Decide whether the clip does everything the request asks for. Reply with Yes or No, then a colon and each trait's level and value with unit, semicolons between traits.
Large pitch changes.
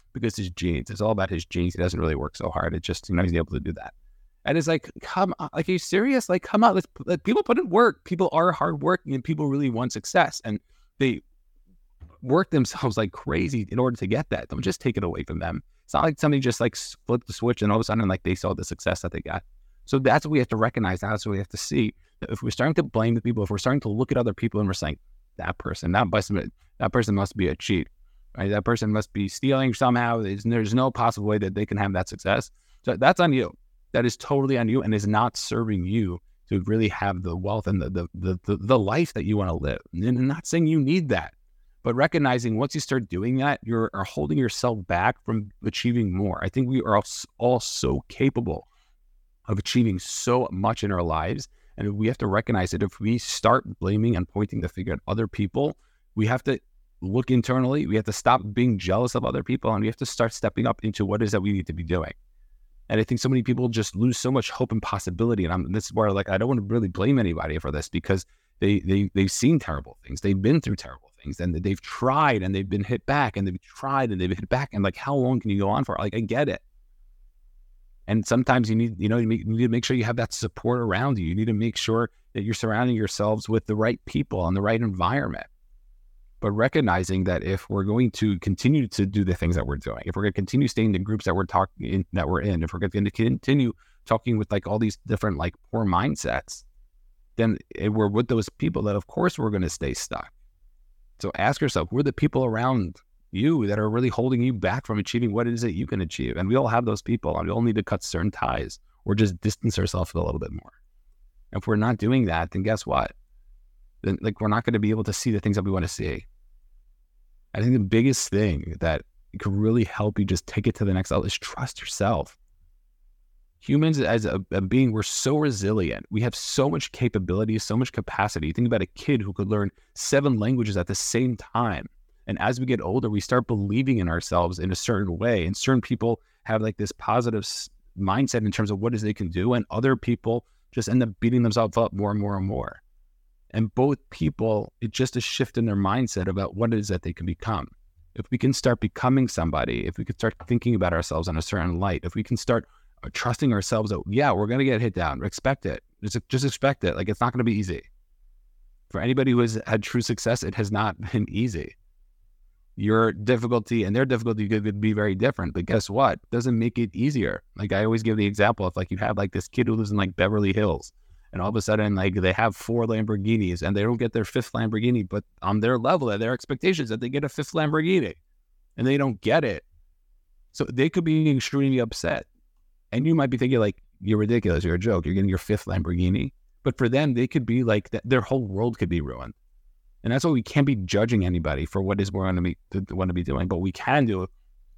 No: average, 4.5 semitones